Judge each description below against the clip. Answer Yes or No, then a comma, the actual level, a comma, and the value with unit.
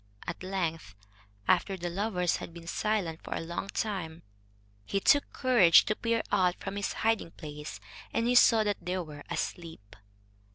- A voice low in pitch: No, medium, 185 Hz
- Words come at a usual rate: Yes, average, 165 wpm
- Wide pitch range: No, average, 4.3 semitones